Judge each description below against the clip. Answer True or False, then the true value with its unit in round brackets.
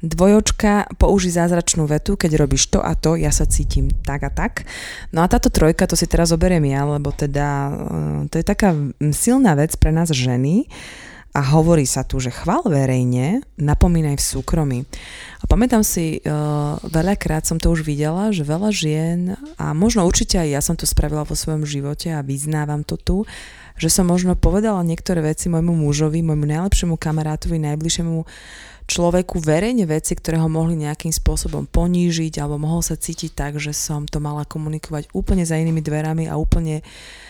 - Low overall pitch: False (160 Hz)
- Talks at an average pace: False (170 wpm)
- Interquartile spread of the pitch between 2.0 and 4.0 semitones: True (2.8 semitones)